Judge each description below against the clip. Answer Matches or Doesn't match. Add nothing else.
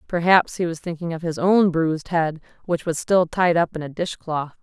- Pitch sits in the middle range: Matches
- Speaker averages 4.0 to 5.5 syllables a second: Matches